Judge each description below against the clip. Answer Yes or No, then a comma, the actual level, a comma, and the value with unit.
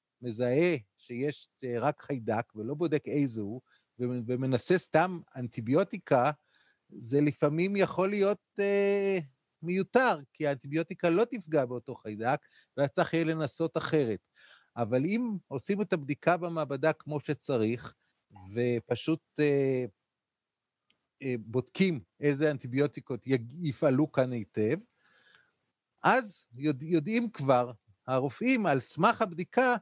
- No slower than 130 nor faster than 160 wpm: No, slow, 100 wpm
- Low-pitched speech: No, medium, 145 Hz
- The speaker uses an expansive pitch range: Yes, wide, 5.8 semitones